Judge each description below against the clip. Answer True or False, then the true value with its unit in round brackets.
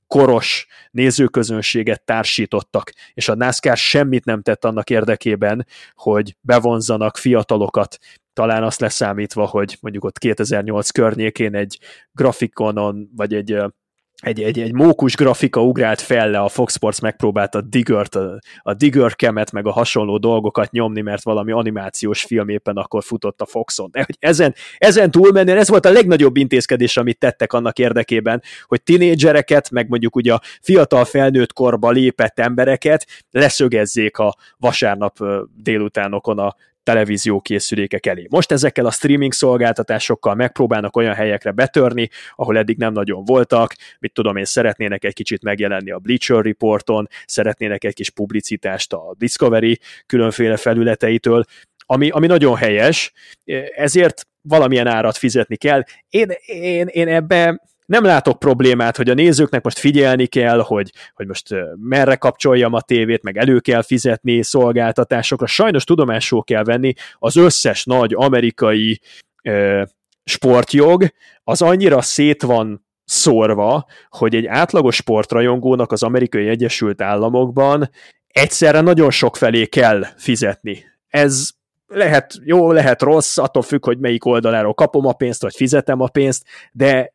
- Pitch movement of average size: True (3.8 semitones)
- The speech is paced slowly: False (140 wpm)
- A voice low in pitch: True (120 Hz)